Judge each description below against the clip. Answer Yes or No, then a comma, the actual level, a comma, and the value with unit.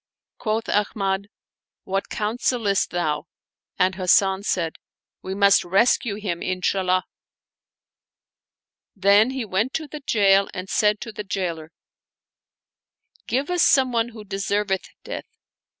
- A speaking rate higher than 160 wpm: No, slow, 135 wpm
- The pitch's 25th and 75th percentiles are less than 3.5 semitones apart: Yes, average, 2.8 semitones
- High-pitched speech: Yes, high, 200 Hz